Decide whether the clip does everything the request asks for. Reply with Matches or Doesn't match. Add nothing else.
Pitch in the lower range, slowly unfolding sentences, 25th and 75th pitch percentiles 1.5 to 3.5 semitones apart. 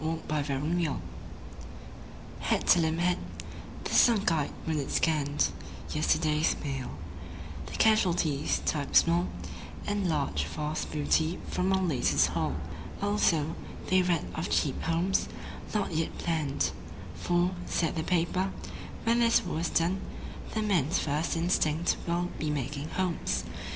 Doesn't match